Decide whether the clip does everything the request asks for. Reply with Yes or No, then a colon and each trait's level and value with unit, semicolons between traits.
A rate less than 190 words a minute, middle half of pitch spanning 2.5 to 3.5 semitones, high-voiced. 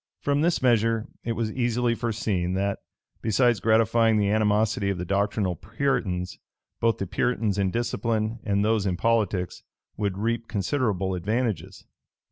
No: average, 140 wpm; average, 2.8 semitones; low, 110 Hz